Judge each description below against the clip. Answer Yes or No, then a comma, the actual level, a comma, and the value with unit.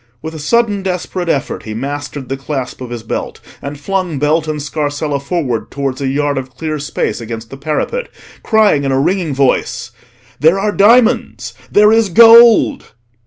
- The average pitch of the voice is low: No, medium, 150 Hz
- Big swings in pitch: Yes, wide, 6.1 semitones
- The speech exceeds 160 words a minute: Yes, average, 170 wpm